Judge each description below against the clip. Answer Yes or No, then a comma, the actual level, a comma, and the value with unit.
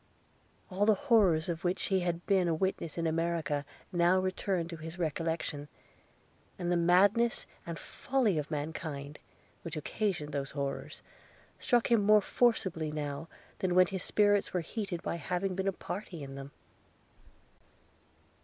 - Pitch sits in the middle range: Yes, medium, 175 Hz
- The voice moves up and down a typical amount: Yes, average, 3.6 semitones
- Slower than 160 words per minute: Yes, average, 150 wpm